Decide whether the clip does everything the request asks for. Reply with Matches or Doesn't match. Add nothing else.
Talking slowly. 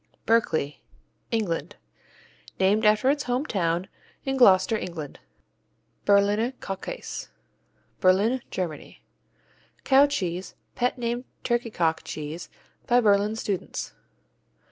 Matches